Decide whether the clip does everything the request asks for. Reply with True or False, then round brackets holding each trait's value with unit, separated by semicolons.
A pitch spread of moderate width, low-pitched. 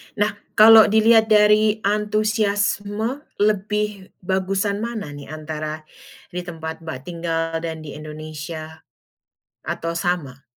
False (4.9 semitones; 190 Hz)